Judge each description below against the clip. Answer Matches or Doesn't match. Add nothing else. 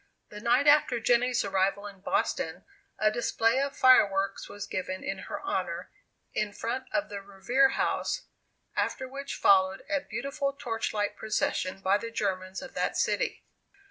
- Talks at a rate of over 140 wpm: Matches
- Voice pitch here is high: Matches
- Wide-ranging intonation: Doesn't match